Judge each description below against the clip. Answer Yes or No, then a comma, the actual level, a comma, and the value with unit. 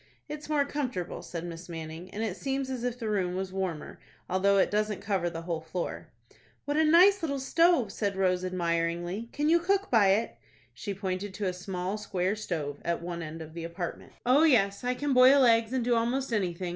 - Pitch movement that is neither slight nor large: No, wide, 6.3 semitones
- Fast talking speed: Yes, fast, 210 wpm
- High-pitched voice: Yes, high, 200 Hz